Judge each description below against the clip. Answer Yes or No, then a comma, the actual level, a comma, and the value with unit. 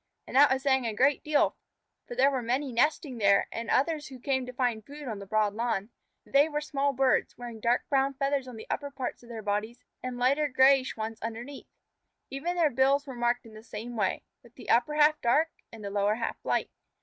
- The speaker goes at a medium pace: No, fast, 220 wpm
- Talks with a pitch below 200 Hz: No, very high, 255 Hz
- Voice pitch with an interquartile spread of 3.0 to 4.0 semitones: Yes, average, 3.5 semitones